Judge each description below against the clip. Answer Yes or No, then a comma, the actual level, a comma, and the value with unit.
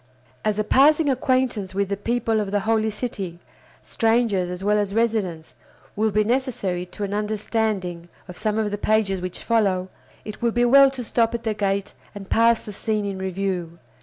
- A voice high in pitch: Yes, high, 210 Hz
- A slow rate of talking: No, average, 190 wpm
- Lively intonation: No, average, 2.8 semitones